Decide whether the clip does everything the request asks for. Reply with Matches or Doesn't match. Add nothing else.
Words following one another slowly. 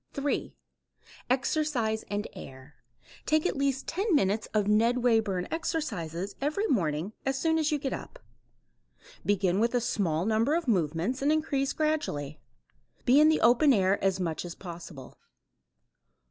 Doesn't match